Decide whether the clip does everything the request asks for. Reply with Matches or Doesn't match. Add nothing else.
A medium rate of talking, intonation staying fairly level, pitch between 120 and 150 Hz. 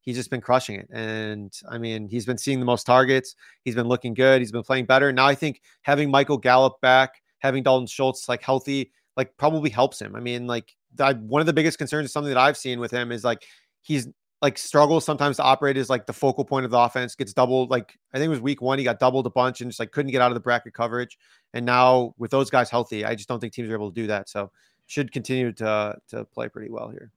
Doesn't match